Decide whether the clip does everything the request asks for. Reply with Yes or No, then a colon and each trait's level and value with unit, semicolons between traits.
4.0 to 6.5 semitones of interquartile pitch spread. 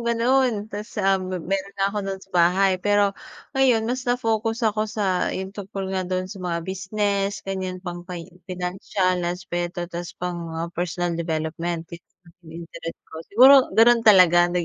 No: average, 3.0 semitones